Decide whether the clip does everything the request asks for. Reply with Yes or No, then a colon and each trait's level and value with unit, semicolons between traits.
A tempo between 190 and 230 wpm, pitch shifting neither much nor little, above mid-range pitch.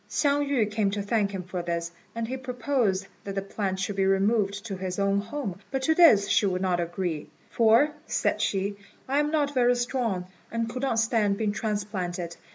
Yes: average, 200 wpm; average, 4.2 semitones; high, 205 Hz